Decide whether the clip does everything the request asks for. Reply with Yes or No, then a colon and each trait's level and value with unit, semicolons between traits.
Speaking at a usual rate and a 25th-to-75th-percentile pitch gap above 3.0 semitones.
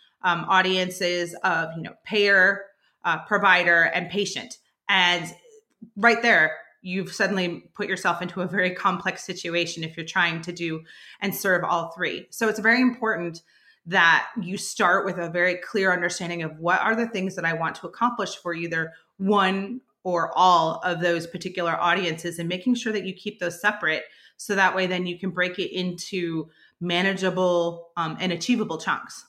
No: average, 170 wpm; narrow, 2.5 semitones